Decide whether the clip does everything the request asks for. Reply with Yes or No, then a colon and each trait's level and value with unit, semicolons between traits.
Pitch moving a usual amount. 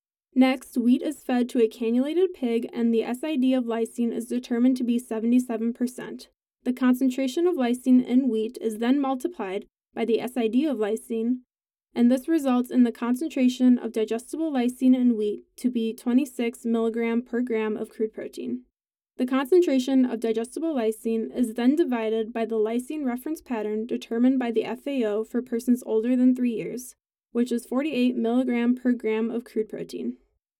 No: narrow, 2.1 semitones